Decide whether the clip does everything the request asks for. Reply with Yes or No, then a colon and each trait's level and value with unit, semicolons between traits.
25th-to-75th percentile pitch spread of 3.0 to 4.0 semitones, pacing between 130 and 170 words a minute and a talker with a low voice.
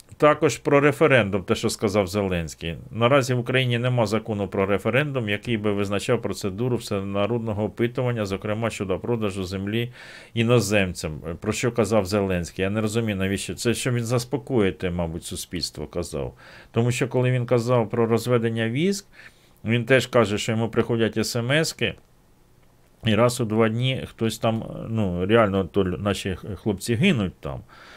Yes: average, 3.3 semitones; average, 150 wpm; low, 110 Hz